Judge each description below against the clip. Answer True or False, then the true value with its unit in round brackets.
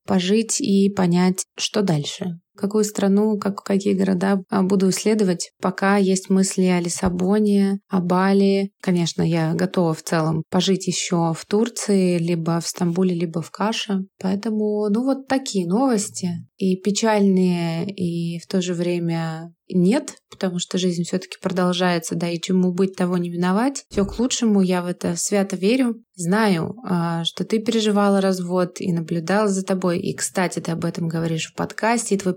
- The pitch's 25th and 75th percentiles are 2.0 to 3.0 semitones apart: True (2.4 semitones)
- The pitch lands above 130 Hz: True (190 Hz)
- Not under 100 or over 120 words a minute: False (160 wpm)